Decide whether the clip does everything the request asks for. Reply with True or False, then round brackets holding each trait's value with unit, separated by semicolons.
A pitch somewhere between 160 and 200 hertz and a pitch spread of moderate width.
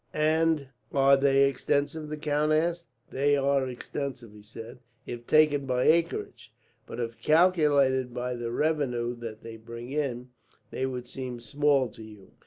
False (135 Hz; 3.8 semitones)